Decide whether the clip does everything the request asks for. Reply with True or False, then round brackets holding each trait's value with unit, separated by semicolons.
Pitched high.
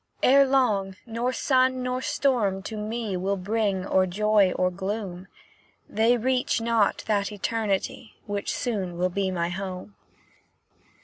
True (210 Hz)